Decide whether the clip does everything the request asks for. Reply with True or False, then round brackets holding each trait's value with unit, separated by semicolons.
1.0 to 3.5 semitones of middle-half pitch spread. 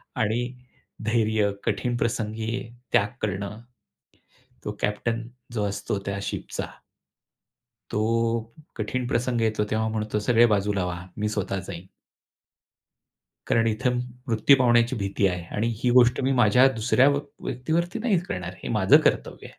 True (2.8 semitones)